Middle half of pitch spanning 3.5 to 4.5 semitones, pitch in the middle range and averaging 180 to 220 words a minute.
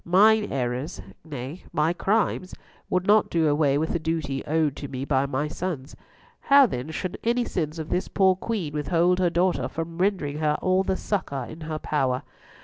Yes: average, 4.1 semitones; medium, 160 Hz; average, 185 wpm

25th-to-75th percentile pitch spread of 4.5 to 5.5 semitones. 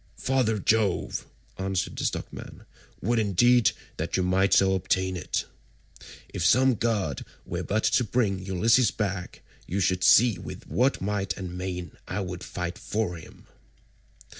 No: average, 3.5 semitones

